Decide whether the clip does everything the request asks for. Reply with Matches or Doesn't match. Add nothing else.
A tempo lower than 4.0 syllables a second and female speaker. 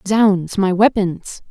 Matches